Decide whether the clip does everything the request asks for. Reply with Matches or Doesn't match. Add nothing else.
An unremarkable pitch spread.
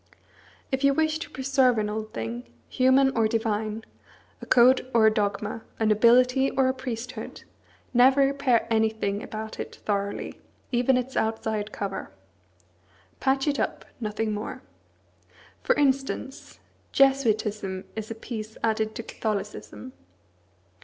Matches